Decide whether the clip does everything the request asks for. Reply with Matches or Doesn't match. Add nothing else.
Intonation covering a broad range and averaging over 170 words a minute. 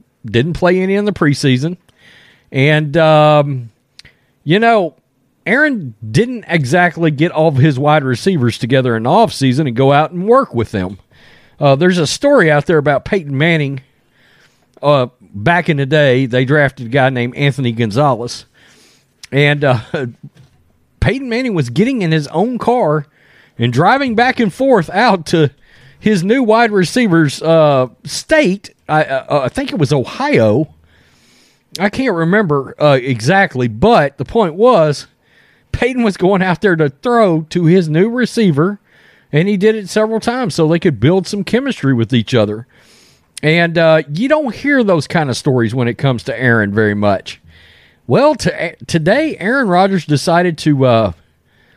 Doesn't match